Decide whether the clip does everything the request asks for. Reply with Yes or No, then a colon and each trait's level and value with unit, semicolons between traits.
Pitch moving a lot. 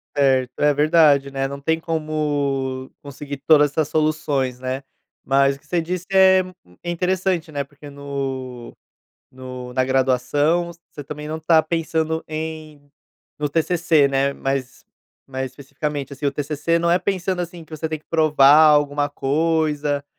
No: average, 2.7 semitones